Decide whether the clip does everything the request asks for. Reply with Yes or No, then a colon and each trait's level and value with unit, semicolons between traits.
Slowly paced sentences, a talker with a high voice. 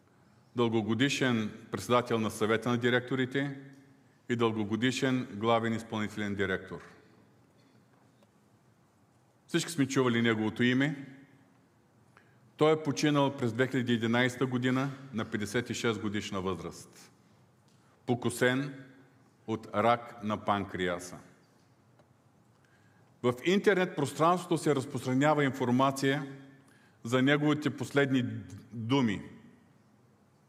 No: slow, 80 wpm; low, 125 Hz